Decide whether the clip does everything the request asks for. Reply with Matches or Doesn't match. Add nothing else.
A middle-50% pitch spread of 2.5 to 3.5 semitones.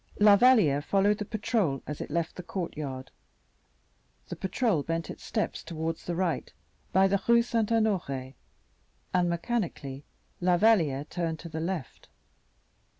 Doesn't match